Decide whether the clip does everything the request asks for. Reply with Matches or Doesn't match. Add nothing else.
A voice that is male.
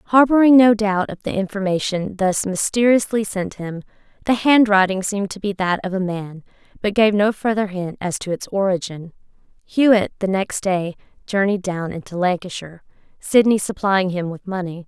Doesn't match